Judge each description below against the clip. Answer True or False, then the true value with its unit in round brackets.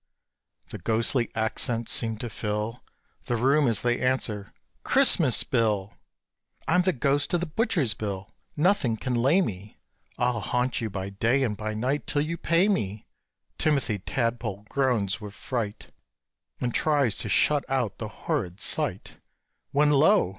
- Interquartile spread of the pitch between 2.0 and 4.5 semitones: False (5.0 semitones)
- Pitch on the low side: True (120 Hz)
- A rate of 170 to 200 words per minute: False (150 wpm)